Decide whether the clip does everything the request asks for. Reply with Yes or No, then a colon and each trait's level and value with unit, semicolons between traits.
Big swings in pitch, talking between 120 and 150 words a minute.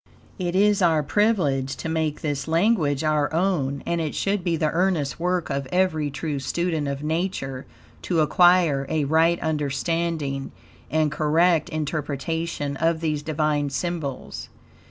No: average, 3.0 semitones; average, 140 wpm